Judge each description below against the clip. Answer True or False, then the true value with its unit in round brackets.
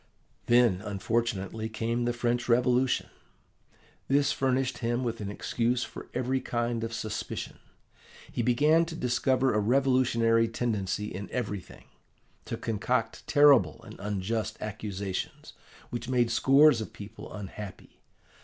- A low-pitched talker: True (115 Hz)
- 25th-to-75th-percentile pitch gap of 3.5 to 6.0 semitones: False (2.8 semitones)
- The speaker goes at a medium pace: False (125 wpm)